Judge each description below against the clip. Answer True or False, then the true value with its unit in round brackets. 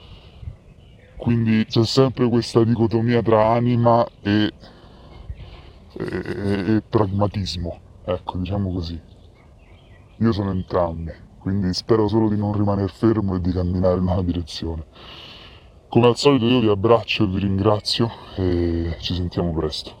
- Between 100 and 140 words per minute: True (130 wpm)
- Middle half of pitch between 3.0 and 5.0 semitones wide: True (3.9 semitones)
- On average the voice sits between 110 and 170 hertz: False (100 Hz)